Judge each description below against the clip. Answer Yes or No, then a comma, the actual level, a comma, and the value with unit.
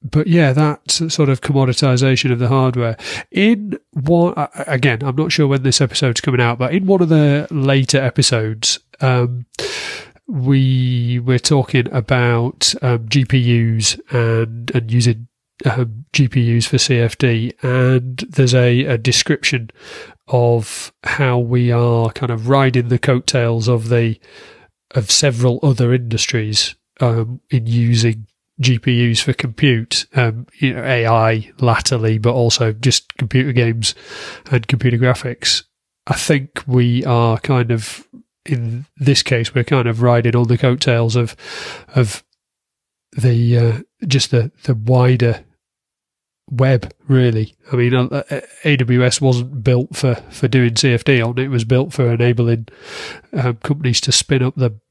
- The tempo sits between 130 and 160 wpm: Yes, average, 140 wpm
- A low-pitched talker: Yes, low, 125 Hz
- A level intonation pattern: Yes, narrow, 2.3 semitones